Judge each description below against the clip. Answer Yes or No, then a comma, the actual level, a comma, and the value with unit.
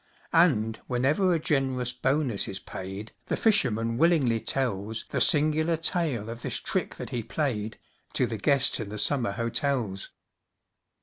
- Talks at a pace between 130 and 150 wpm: Yes, average, 145 wpm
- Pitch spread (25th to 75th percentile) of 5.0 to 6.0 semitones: Yes, average, 5.3 semitones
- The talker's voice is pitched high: No, low, 125 Hz